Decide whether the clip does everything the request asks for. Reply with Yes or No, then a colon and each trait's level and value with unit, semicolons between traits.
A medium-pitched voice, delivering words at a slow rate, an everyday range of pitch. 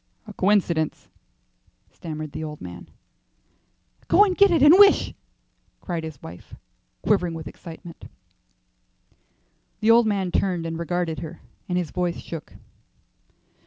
Yes: medium, 175 Hz; slow, 125 wpm; average, 4.2 semitones